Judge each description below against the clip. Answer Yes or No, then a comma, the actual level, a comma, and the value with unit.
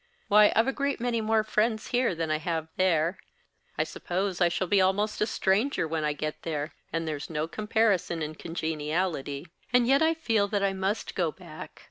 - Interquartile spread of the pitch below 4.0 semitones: No, average, 5.3 semitones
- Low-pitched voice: No, medium, 185 Hz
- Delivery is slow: No, average, 195 wpm